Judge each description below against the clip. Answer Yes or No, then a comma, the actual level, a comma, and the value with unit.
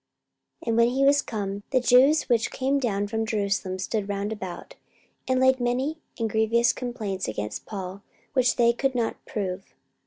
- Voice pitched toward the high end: Yes, high, 230 Hz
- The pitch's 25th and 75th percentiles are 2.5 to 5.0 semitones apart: Yes, average, 4.1 semitones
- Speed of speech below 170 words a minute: No, average, 175 wpm